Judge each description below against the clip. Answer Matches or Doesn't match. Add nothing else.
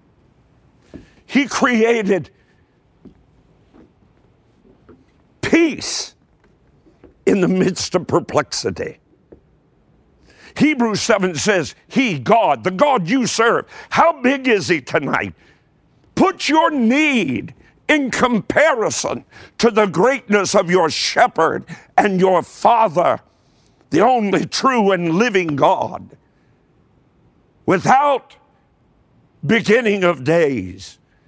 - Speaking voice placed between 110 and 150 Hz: Doesn't match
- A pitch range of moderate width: Doesn't match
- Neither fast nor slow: Doesn't match